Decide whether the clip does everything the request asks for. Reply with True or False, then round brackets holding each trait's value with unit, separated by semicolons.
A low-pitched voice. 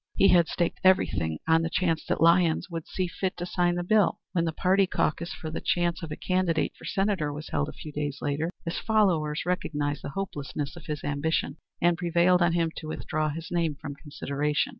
False (165 Hz)